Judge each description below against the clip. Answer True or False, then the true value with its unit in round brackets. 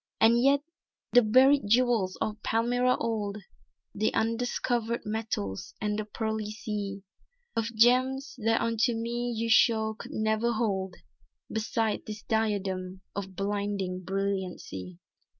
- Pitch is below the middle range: False (220 Hz)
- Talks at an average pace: False (120 wpm)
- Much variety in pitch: False (2.7 semitones)